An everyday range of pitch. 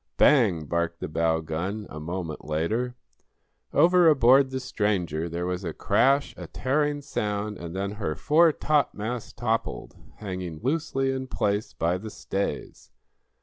No: wide, 7.5 semitones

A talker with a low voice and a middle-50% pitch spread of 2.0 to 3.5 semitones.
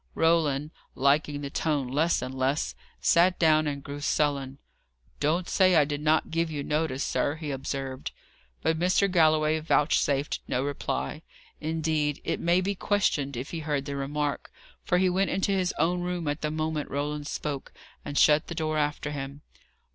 No: medium, 150 Hz; narrow, 2.4 semitones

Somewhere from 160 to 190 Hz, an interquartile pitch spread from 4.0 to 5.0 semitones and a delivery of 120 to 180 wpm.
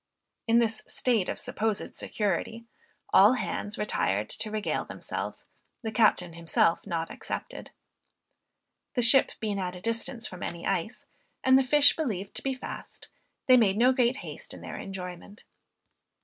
No: high, 215 Hz; average, 4.6 semitones; average, 150 wpm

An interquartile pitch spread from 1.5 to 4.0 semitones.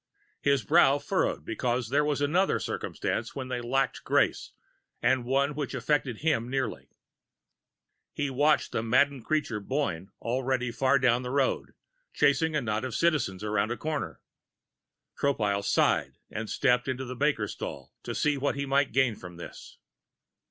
Yes: average, 3.5 semitones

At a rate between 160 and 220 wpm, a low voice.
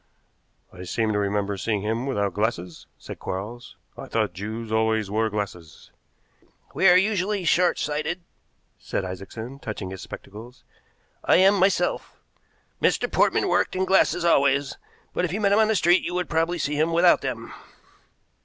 Yes: average, 165 wpm; low, 125 Hz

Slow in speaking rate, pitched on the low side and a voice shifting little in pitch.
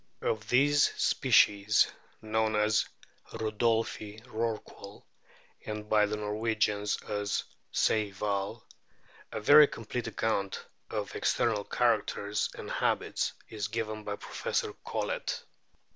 Yes: slow, 100 wpm; low, 110 Hz; narrow, 1.3 semitones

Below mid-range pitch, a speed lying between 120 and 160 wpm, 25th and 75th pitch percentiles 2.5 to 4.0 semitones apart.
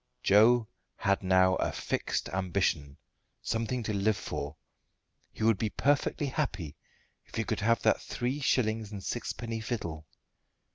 Yes: low, 110 Hz; average, 140 wpm; average, 3.7 semitones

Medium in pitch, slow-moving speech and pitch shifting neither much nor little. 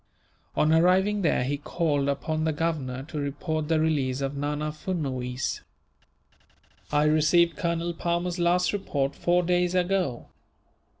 Yes: medium, 155 Hz; slow, 130 wpm; average, 3.4 semitones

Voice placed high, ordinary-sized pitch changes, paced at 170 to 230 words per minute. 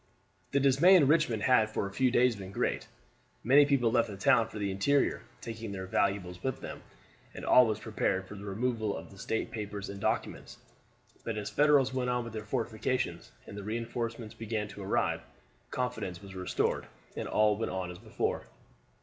No: low, 110 Hz; average, 3.9 semitones; average, 190 wpm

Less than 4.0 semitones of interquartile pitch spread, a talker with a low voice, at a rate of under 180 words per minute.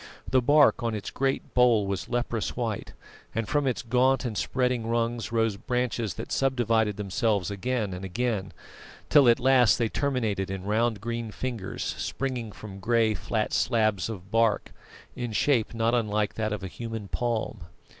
Yes: average, 2.8 semitones; low, 115 Hz; average, 165 wpm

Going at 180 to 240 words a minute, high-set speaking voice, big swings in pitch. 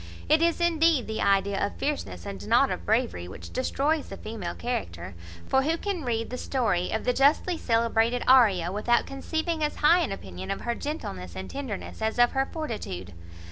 Yes: average, 185 wpm; high, 240 Hz; wide, 7.9 semitones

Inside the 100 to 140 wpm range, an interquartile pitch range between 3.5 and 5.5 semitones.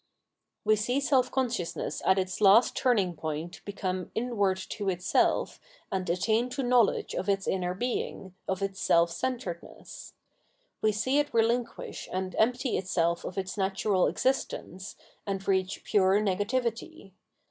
Yes: slow, 135 wpm; average, 4.2 semitones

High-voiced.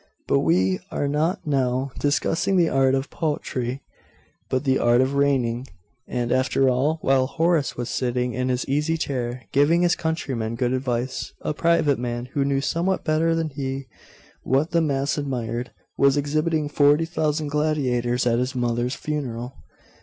No: low, 135 Hz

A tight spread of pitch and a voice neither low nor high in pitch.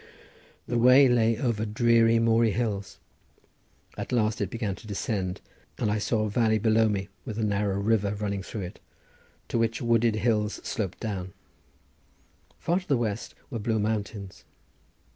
No: narrow, 2.1 semitones; low, 110 Hz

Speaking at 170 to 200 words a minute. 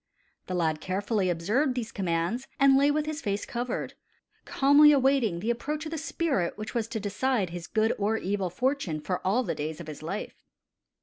Yes: average, 190 wpm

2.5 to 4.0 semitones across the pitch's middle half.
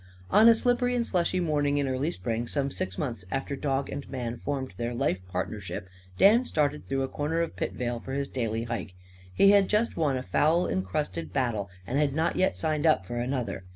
No: average, 5.2 semitones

